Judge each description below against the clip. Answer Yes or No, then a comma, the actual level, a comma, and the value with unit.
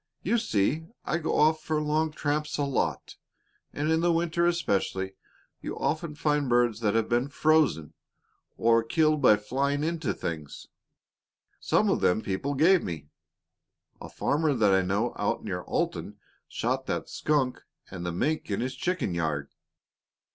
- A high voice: No, medium, 140 Hz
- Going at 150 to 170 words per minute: Yes, average, 155 wpm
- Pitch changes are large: Yes, wide, 6.9 semitones